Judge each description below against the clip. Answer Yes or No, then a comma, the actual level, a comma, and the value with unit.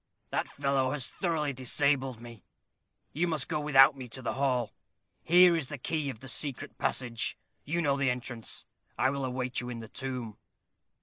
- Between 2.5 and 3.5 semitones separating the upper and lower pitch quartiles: Yes, average, 2.8 semitones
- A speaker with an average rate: Yes, average, 180 wpm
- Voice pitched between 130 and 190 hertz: Yes, low, 135 Hz